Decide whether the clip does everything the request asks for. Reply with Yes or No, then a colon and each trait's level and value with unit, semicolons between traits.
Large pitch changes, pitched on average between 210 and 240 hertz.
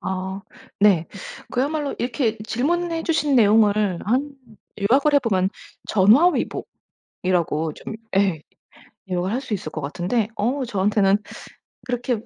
Yes: wide, 5.7 semitones; high, 220 Hz